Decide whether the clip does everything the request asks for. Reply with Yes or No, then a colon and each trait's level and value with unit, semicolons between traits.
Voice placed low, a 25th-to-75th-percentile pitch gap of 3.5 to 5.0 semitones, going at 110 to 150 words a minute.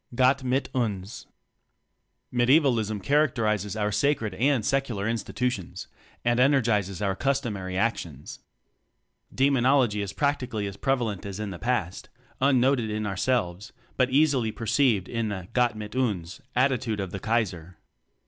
Yes: low, 115 Hz; average, 4.4 semitones; slow, 135 wpm